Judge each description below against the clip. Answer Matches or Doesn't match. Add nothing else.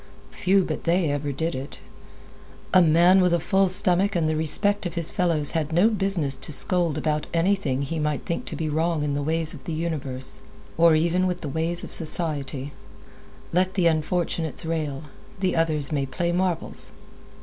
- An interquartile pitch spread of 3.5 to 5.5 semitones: Doesn't match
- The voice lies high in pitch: Doesn't match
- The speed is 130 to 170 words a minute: Doesn't match